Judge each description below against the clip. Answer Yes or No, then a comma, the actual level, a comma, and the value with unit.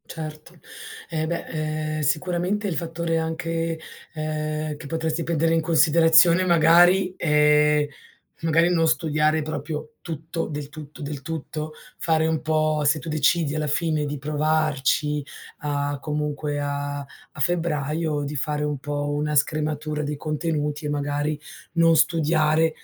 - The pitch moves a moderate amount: No, narrow, 1.6 semitones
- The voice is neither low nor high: Yes, medium, 155 Hz